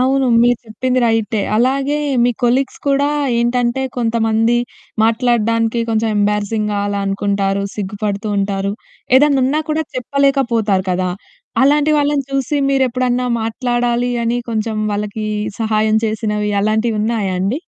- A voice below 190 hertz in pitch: No, high, 230 Hz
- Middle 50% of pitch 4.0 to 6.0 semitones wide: No, average, 3.3 semitones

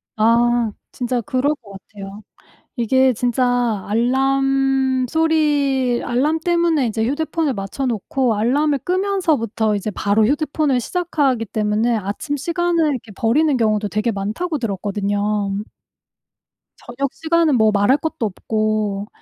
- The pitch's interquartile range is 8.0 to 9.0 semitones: No, average, 5.1 semitones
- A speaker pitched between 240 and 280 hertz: Yes, very high, 250 Hz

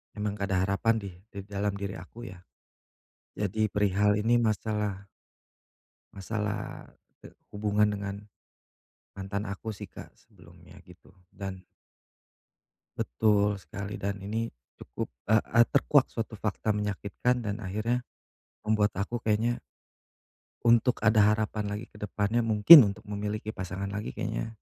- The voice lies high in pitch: No, low, 105 Hz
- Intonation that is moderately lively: No, narrow, 1.7 semitones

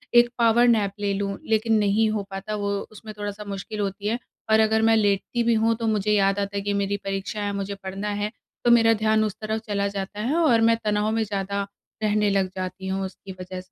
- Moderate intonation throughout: No, narrow, 1.8 semitones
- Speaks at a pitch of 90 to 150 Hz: No, high, 205 Hz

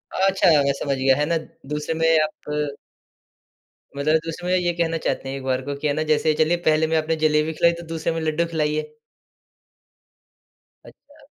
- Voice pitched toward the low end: No, medium, 155 Hz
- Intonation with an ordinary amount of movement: No, narrow, 1.8 semitones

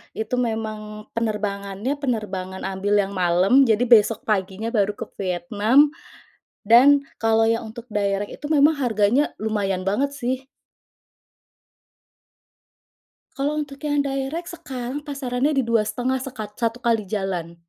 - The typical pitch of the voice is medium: No, high, 225 Hz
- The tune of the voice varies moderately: Yes, average, 4.6 semitones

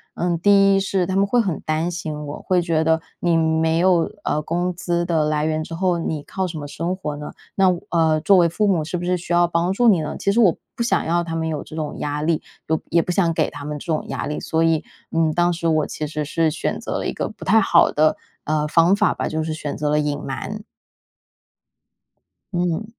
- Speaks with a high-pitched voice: No, medium, 165 Hz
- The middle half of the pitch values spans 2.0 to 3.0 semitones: Yes, narrow, 2.4 semitones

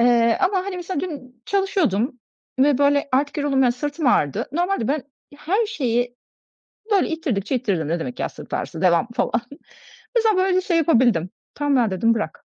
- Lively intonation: Yes, wide, 6.7 semitones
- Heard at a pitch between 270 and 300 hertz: Yes, very high, 275 Hz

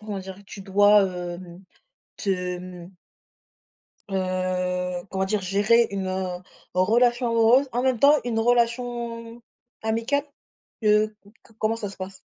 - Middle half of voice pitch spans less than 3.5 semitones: No, average, 3.9 semitones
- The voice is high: Yes, high, 205 Hz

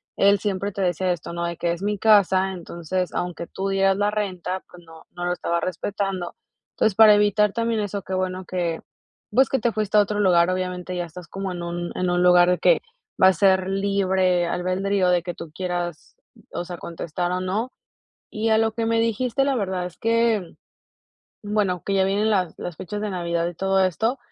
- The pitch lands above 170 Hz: Yes, high, 190 Hz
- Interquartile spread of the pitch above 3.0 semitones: No, average, 2.7 semitones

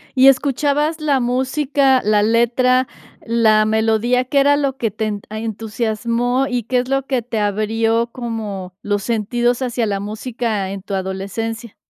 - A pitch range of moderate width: Yes, average, 3.1 semitones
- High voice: Yes, high, 230 Hz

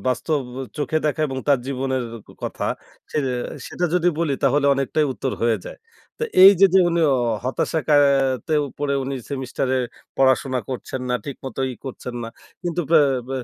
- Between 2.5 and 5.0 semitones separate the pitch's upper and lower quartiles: Yes, average, 2.9 semitones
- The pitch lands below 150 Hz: Yes, low, 135 Hz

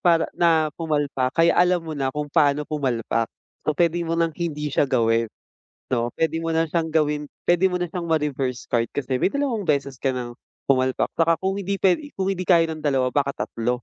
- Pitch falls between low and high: Yes, medium, 155 Hz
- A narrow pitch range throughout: No, average, 4.2 semitones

